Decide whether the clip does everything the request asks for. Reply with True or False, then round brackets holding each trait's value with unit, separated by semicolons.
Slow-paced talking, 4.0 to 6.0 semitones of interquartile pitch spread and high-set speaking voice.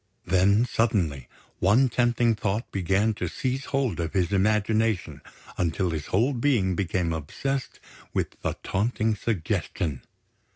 False (125 wpm; 4.6 semitones; 105 Hz)